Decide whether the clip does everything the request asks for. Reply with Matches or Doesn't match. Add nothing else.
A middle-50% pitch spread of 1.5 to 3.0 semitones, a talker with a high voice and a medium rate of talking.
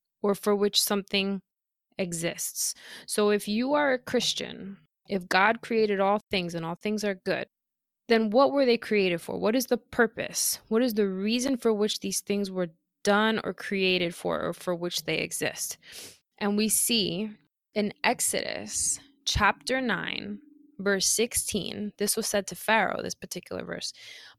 Matches